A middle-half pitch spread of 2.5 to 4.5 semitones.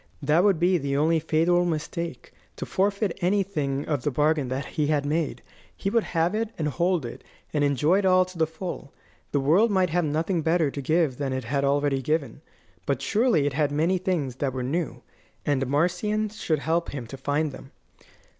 Yes: average, 4.0 semitones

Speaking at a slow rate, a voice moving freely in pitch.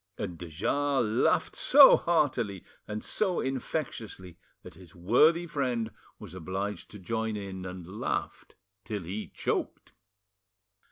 Yes: slow, 125 wpm; wide, 6.3 semitones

